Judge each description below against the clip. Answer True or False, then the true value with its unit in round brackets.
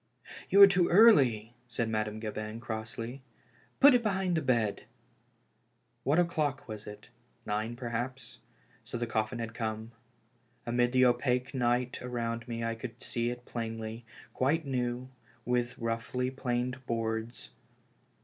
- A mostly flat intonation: True (2.1 semitones)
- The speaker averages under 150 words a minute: True (140 wpm)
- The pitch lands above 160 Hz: False (120 Hz)